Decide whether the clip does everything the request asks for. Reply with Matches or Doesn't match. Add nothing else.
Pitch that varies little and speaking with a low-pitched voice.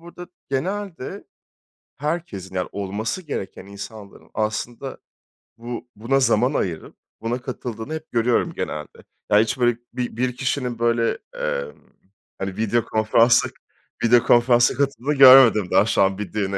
Doesn't match